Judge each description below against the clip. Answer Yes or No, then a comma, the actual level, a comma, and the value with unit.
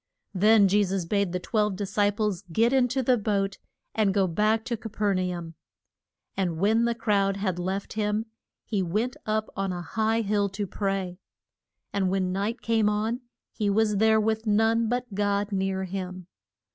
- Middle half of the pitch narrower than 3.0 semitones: Yes, narrow, 2.4 semitones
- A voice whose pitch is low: No, high, 205 Hz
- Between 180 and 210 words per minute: Yes, average, 185 wpm